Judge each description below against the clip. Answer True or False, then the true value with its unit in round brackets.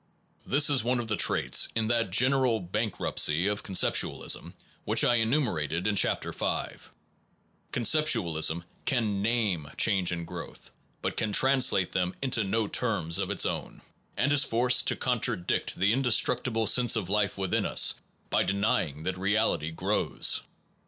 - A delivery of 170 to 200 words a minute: False (150 wpm)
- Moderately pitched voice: False (110 Hz)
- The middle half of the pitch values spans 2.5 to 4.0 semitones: False (4.8 semitones)